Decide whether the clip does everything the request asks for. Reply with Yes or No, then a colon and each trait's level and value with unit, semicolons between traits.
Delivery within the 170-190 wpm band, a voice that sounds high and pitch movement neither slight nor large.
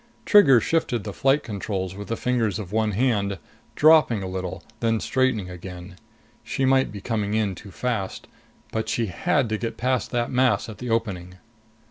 No: average, 175 wpm; low, 110 Hz; average, 4.2 semitones